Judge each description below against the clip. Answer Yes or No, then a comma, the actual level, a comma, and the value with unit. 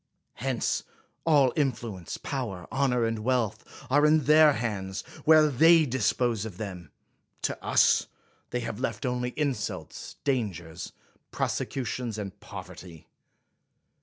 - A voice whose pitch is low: Yes, low, 120 Hz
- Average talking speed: No, slow, 125 wpm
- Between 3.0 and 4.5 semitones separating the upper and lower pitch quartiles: No, average, 5.1 semitones